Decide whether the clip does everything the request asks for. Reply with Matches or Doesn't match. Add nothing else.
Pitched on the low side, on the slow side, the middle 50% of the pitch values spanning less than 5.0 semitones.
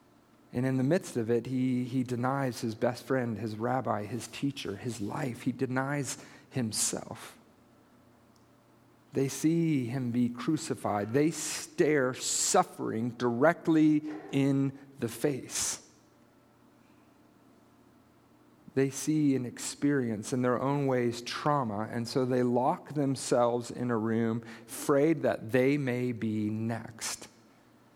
Matches